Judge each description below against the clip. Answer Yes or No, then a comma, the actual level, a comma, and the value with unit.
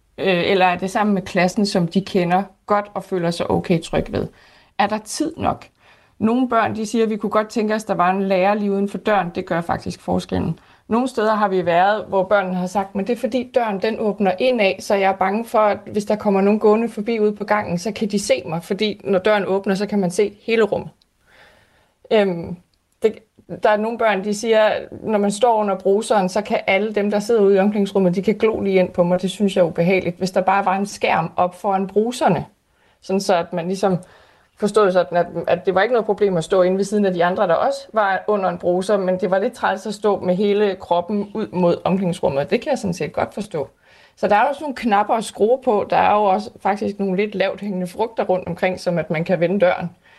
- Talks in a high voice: Yes, high, 200 Hz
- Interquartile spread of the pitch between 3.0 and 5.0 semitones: No, narrow, 2.5 semitones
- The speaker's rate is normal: No, fast, 245 wpm